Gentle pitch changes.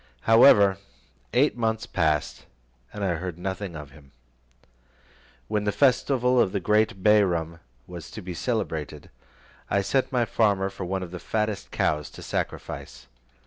No: average, 4.2 semitones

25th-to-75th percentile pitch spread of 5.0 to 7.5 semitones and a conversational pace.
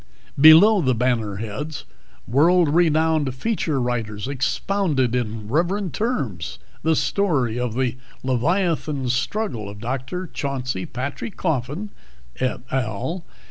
No: wide, 5.5 semitones; slow, 110 wpm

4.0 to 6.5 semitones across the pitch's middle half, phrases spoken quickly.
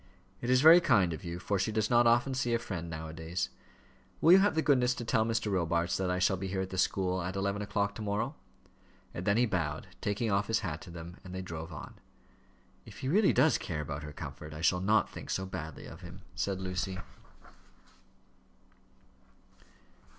Yes: average, 4.7 semitones; fast, 210 wpm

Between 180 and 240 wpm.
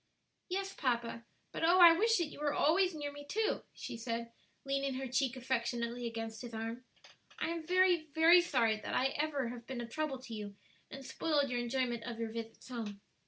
Yes: average, 200 wpm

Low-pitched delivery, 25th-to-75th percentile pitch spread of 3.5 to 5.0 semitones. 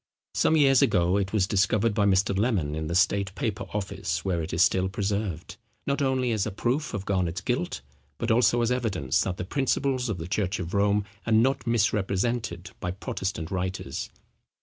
Yes: low, 100 Hz; average, 4.0 semitones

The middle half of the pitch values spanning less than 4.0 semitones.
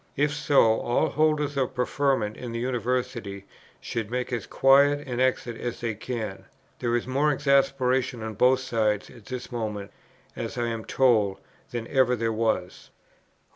Yes: average, 2.8 semitones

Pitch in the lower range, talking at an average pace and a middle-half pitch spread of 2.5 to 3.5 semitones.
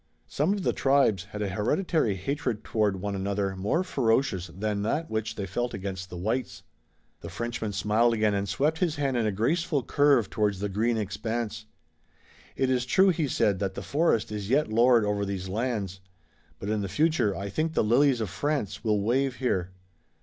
No: low, 110 Hz; average, 190 wpm; average, 5.1 semitones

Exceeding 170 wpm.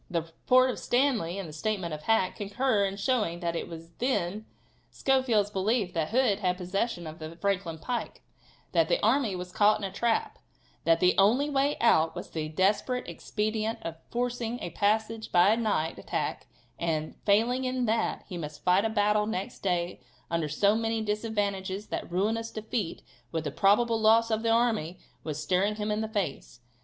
Yes: average, 185 wpm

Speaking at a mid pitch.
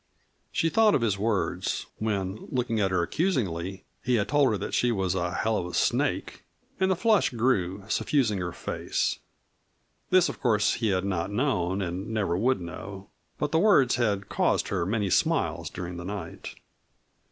No: low, 105 Hz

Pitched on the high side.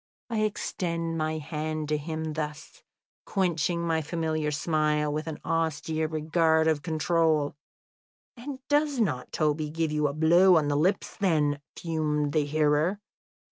No: medium, 155 Hz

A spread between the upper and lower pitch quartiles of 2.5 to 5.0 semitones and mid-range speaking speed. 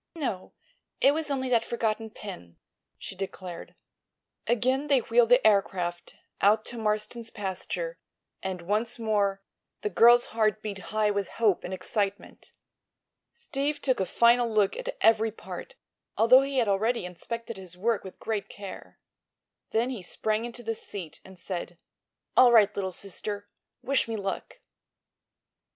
Yes: average, 3.4 semitones; average, 145 wpm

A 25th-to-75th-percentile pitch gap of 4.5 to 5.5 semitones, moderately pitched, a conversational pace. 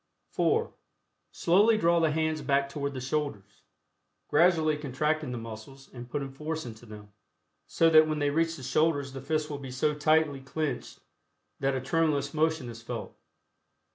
No: average, 3.0 semitones; medium, 145 Hz; average, 165 wpm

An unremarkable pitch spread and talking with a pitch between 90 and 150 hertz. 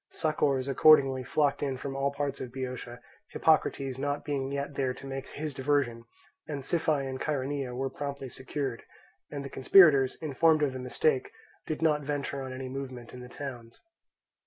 No: narrow, 1.9 semitones; low, 135 Hz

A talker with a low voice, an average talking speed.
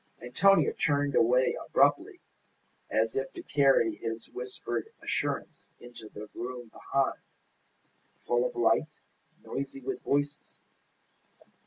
No: low, 125 Hz; slow, 110 wpm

